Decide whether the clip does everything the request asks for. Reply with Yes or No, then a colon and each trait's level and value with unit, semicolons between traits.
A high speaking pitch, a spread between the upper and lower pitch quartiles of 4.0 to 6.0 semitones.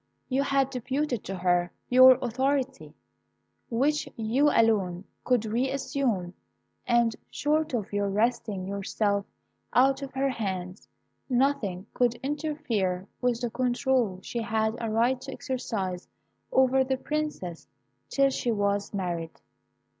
Yes: high, 240 Hz; average, 4.8 semitones